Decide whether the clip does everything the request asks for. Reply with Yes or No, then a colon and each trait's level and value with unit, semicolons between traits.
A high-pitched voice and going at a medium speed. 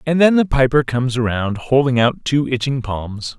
No: low, 130 Hz; average, 195 wpm